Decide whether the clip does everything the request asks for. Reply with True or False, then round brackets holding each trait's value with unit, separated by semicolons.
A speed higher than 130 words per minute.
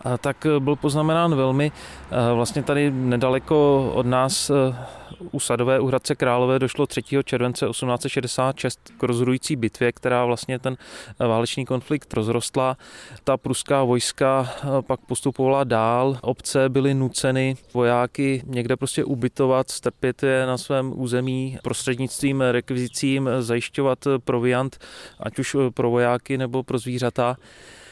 False (120 wpm)